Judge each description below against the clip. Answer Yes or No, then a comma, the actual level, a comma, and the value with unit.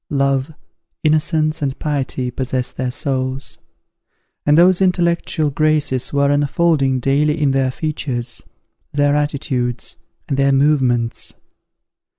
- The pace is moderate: No, slow, 110 wpm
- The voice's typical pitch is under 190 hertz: Yes, medium, 140 Hz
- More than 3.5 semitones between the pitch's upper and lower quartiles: No, average, 2.7 semitones